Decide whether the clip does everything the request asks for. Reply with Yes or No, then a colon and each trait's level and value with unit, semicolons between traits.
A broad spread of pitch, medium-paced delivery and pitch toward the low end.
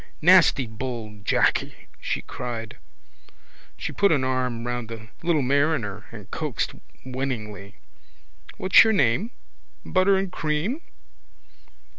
No: wide, 6.6 semitones; slow, 110 wpm; low, 130 Hz